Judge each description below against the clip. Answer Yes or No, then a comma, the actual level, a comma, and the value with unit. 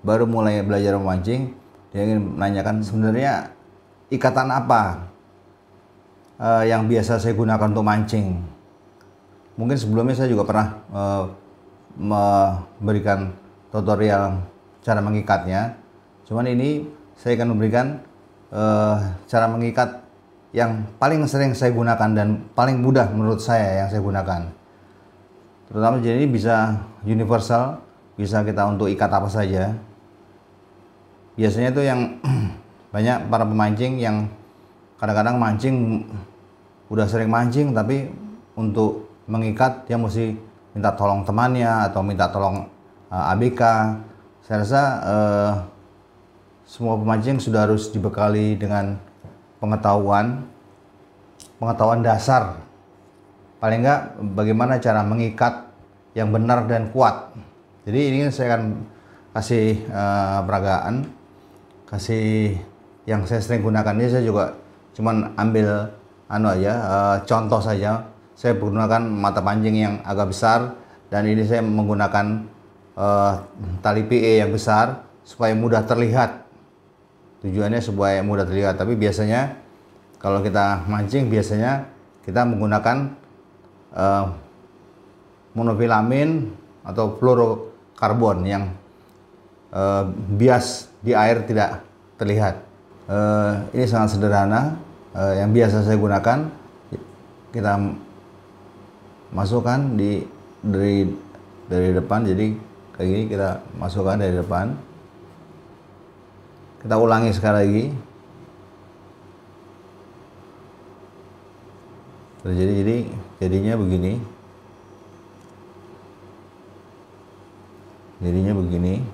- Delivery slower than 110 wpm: Yes, average, 100 wpm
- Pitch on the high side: No, low, 105 Hz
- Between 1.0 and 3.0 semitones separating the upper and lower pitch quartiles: Yes, narrow, 2.6 semitones